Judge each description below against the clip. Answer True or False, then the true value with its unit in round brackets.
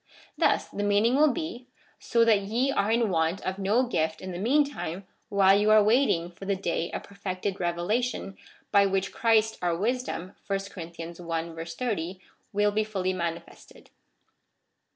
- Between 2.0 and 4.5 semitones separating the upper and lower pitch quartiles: True (4.2 semitones)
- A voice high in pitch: True (200 Hz)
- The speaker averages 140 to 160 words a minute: True (155 wpm)